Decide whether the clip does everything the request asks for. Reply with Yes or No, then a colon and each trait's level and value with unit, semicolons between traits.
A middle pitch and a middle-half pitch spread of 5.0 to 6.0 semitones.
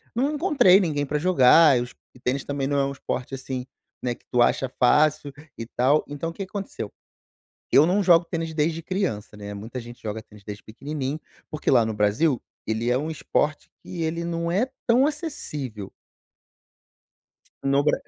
Yes: medium, 145 Hz; wide, 5.4 semitones